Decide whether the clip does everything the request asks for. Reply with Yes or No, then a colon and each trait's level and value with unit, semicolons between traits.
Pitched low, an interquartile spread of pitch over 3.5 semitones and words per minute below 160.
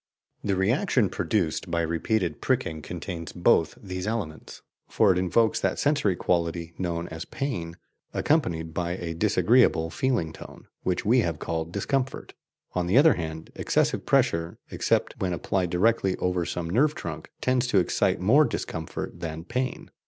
Yes: very low, 90 Hz; average, 5.3 semitones; average, 150 wpm